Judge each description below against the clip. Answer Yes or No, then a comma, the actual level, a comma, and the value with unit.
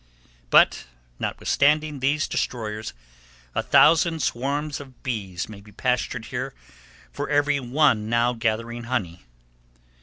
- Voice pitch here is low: Yes, low, 125 Hz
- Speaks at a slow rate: Yes, slow, 115 wpm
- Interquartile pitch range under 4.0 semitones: No, average, 4.6 semitones